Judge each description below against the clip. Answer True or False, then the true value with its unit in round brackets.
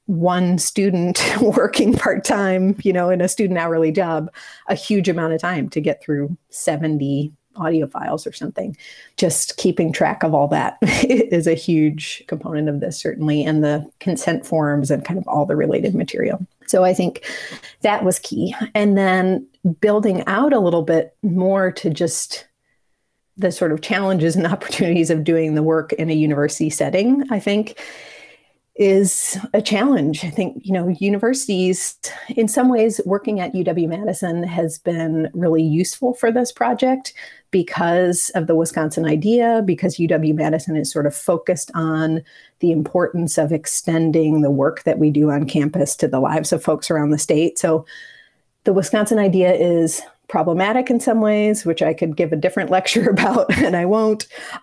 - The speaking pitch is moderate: True (175 Hz)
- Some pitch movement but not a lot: True (3.8 semitones)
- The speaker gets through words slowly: False (170 wpm)